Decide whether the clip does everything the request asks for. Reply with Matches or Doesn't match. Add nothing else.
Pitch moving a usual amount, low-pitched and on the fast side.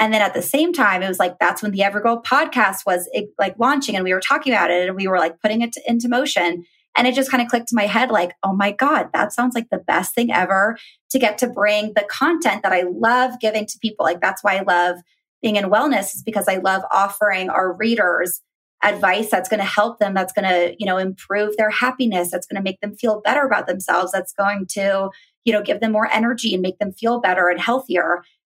Doesn't match